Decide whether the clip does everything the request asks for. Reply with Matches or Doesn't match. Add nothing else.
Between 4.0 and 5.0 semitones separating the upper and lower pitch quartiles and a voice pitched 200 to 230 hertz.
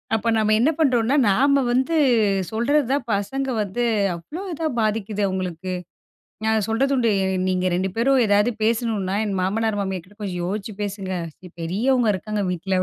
Matches